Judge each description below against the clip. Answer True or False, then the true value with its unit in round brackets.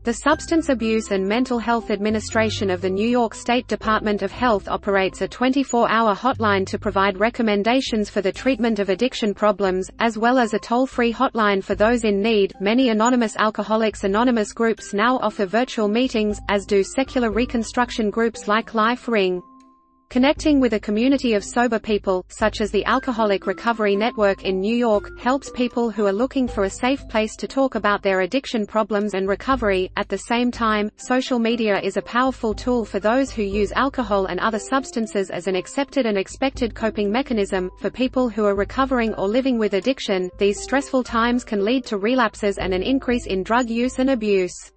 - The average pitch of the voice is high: True (220 Hz)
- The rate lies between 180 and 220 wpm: True (185 wpm)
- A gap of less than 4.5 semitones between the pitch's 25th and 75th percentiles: True (3.5 semitones)